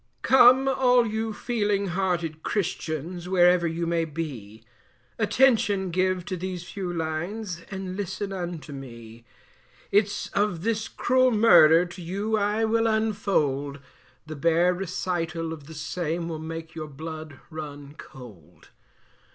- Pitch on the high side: No, medium, 175 Hz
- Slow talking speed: Yes, slow, 130 wpm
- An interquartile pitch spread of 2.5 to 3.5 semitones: No, average, 4.5 semitones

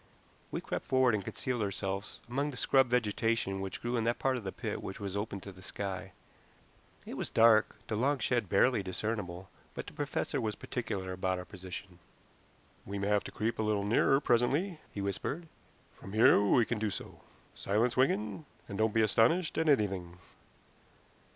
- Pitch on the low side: Yes, low, 110 Hz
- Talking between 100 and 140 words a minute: No, average, 185 wpm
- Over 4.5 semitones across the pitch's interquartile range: No, average, 3.9 semitones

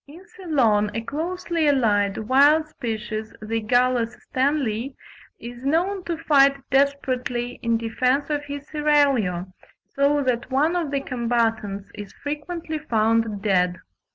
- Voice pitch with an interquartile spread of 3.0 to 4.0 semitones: No, average, 4.7 semitones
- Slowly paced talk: Yes, slow, 125 wpm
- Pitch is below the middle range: No, very high, 255 Hz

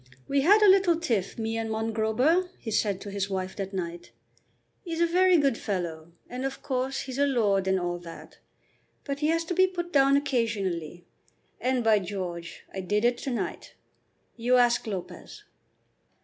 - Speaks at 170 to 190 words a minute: Yes, average, 175 wpm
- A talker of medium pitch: No, high, 230 Hz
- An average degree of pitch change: No, wide, 6.5 semitones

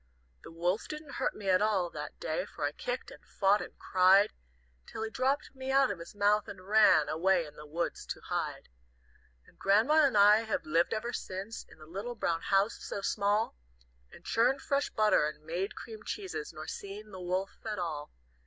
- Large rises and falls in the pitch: No, average, 3.9 semitones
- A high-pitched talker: Yes, high, 205 Hz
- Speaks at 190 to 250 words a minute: Yes, average, 200 wpm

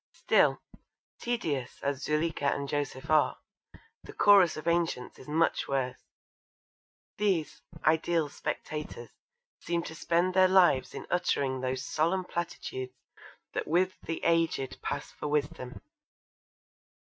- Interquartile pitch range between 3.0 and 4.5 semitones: Yes, average, 3.8 semitones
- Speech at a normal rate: No, slow, 120 wpm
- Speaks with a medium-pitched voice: Yes, medium, 155 Hz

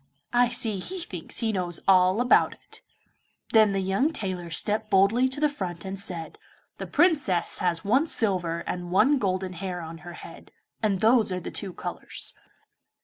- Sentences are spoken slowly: No, average, 175 wpm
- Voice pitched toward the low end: No, high, 195 Hz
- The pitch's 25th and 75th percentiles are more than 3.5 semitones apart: Yes, average, 4.2 semitones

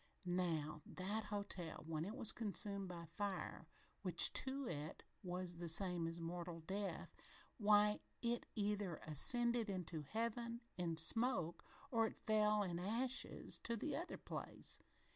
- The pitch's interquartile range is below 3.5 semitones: No, average, 4.6 semitones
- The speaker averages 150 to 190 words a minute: No, average, 140 wpm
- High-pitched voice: Yes, high, 195 Hz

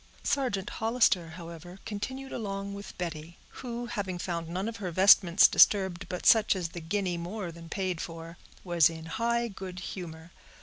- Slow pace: No, average, 165 wpm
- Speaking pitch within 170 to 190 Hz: Yes, medium, 185 Hz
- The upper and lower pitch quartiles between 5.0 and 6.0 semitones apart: No, average, 3.5 semitones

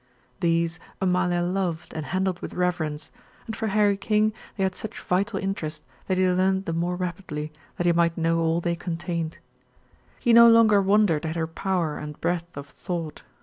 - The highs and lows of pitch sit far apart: No, narrow, 2.6 semitones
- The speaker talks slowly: No, average, 180 wpm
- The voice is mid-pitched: Yes, medium, 175 Hz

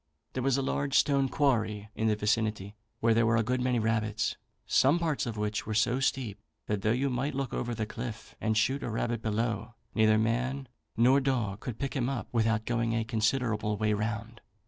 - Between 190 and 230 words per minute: Yes, fast, 205 wpm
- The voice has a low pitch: Yes, low, 115 Hz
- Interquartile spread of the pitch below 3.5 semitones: Yes, average, 2.8 semitones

